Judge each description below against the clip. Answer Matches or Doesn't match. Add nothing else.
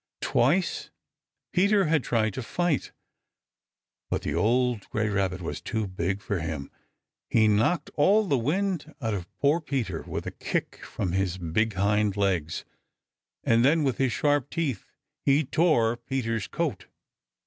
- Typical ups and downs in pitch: Doesn't match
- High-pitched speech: Doesn't match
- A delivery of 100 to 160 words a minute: Matches